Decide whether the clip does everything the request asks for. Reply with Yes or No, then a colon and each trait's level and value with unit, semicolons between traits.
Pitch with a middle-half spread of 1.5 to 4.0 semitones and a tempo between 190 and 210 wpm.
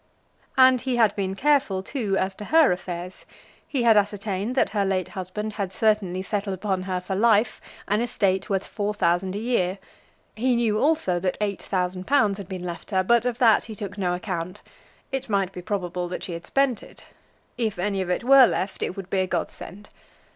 Yes: average, 3.3 semitones; fast, 205 wpm